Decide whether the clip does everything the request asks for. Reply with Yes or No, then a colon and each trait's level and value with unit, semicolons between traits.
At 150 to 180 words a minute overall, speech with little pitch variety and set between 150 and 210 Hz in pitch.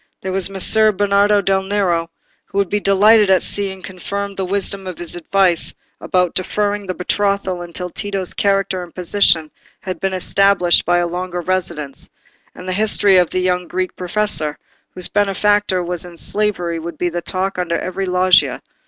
Yes: average, 170 wpm; narrow, 2.1 semitones; medium, 185 Hz